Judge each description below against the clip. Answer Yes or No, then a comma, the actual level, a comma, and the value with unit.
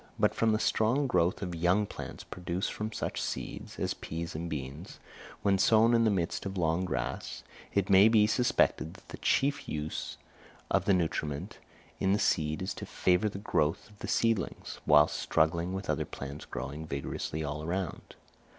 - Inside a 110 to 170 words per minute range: No, average, 180 wpm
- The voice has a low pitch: Yes, very low, 90 Hz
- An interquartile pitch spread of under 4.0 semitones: No, average, 4.8 semitones